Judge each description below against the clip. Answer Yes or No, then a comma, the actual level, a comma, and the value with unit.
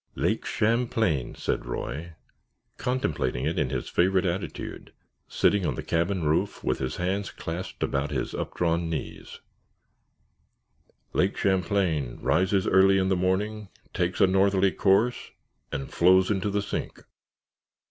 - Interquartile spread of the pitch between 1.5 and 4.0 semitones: Yes, average, 3.1 semitones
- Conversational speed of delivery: No, slow, 130 wpm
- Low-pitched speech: Yes, very low, 95 Hz